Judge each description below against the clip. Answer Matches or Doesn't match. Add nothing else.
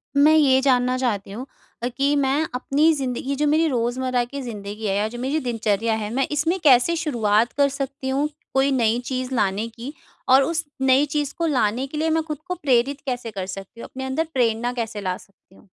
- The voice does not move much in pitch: Doesn't match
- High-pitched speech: Matches